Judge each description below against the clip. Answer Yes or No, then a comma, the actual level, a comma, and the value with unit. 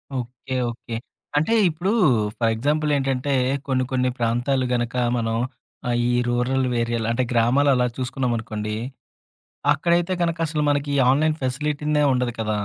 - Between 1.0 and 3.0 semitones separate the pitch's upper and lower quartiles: No, average, 3.7 semitones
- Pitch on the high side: No, low, 130 Hz